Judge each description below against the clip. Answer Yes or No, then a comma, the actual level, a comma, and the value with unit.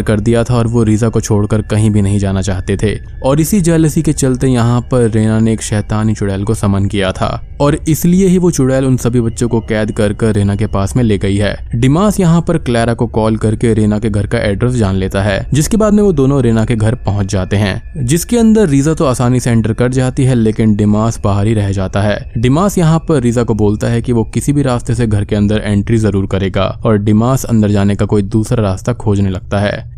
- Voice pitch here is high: No, low, 115 Hz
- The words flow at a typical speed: No, fast, 245 wpm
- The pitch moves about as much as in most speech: Yes, average, 3.6 semitones